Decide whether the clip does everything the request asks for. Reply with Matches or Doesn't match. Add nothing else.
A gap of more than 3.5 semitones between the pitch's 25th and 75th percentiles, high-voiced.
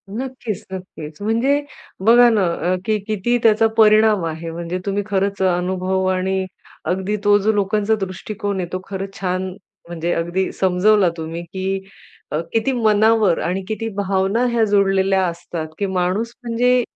Doesn't match